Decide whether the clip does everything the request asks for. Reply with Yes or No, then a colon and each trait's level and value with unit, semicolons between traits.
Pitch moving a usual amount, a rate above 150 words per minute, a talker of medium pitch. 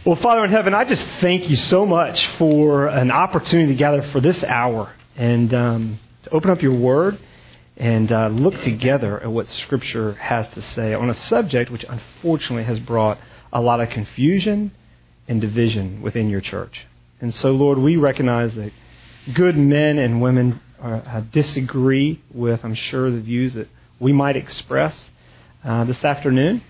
No: average, 4.1 semitones; average, 170 wpm; low, 125 Hz